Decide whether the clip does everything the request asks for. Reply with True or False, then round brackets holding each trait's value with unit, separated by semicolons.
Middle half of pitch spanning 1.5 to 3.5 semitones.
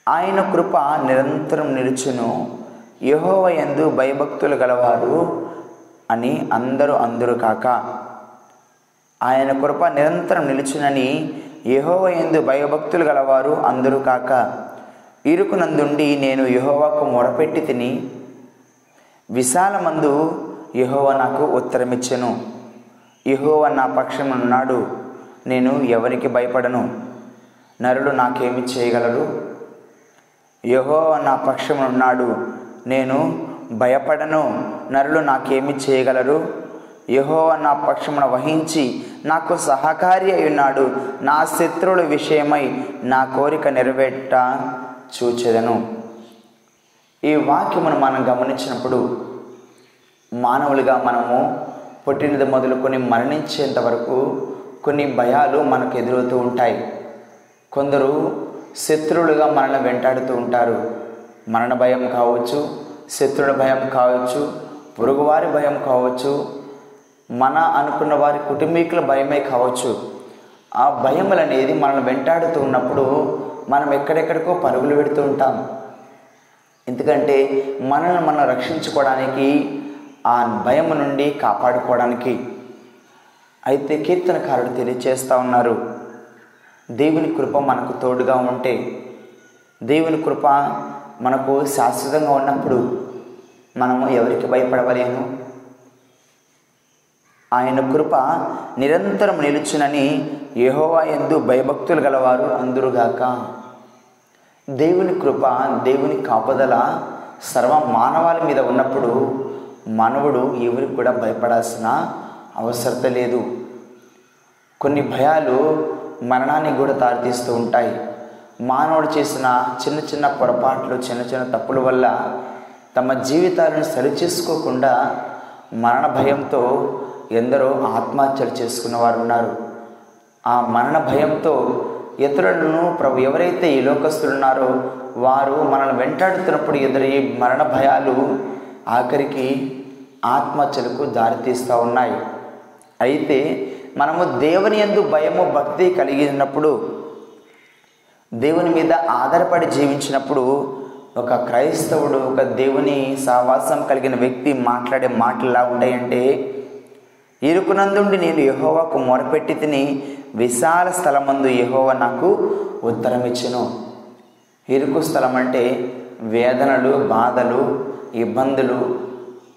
True (2.8 semitones)